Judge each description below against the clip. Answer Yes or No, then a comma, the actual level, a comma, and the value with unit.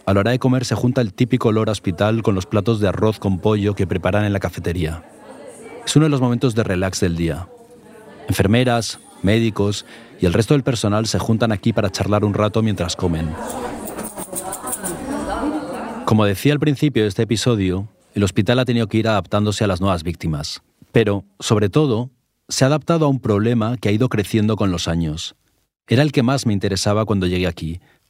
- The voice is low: Yes, low, 105 Hz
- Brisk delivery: Yes, fast, 195 wpm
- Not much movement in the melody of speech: No, average, 3.6 semitones